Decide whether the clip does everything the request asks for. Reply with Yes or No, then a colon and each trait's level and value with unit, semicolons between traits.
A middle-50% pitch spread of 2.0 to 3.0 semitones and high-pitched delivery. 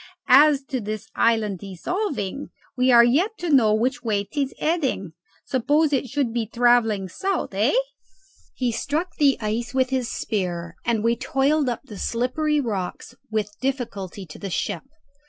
No: average, 4.6 semitones; high, 240 Hz